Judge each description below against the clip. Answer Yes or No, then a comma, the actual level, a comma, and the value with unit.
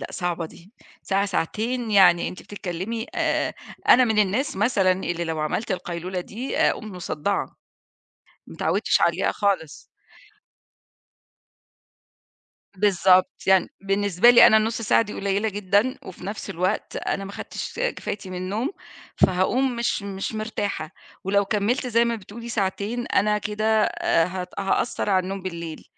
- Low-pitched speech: No, high, 200 Hz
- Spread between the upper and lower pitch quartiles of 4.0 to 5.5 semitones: No, average, 3.1 semitones